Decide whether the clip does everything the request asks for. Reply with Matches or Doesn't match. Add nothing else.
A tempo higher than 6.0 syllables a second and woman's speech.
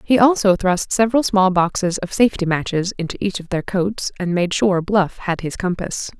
Doesn't match